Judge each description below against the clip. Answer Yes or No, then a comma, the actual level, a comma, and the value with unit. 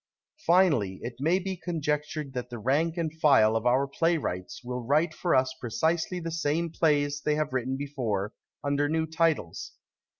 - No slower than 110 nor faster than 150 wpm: No, average, 170 wpm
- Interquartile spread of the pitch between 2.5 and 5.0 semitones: Yes, average, 4.4 semitones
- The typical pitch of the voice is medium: Yes, medium, 145 Hz